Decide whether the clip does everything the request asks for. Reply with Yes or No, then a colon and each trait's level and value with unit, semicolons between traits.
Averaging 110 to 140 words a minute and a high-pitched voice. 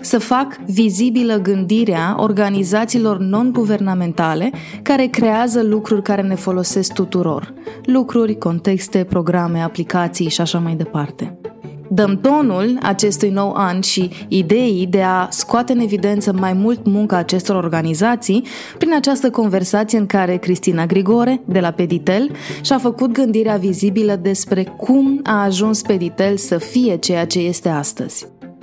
Yes: average, 130 wpm; high, 200 Hz